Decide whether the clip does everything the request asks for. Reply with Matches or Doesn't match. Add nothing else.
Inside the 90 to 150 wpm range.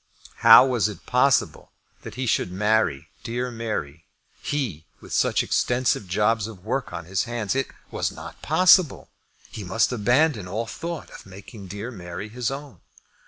Doesn't match